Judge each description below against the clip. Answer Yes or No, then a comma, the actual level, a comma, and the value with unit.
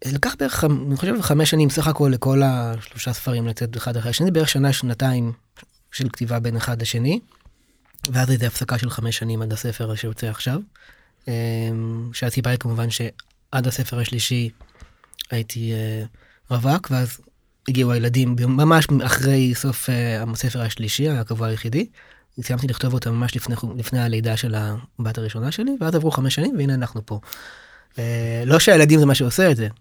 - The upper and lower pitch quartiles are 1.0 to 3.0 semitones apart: Yes, average, 2.7 semitones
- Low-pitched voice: Yes, low, 125 Hz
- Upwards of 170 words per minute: No, average, 155 wpm